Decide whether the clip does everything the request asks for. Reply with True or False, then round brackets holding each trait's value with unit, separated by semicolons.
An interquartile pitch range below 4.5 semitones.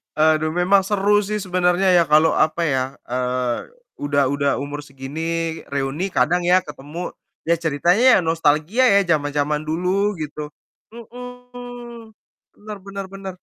False (5.3 semitones)